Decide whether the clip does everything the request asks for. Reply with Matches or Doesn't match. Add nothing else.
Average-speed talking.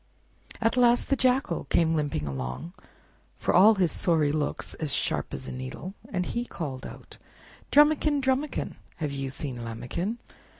Matches